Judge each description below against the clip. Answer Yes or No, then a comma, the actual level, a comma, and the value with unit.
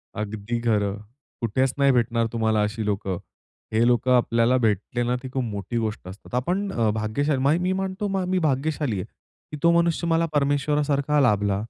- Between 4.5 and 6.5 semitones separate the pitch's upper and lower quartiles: Yes, average, 5.3 semitones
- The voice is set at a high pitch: No, low, 120 Hz